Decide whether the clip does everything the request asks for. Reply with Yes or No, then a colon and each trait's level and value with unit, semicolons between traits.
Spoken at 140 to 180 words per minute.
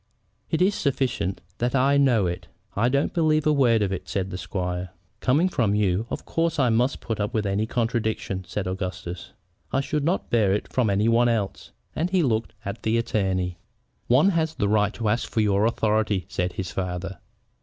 No: average, 200 wpm